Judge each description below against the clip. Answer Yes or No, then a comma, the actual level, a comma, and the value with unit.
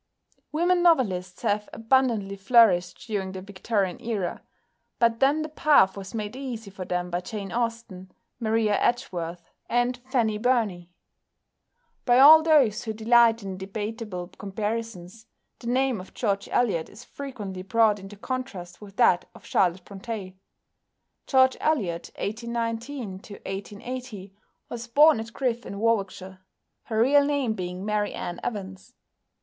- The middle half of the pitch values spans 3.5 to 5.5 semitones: Yes, average, 4.1 semitones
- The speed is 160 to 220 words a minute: No, slow, 135 wpm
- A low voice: No, high, 220 Hz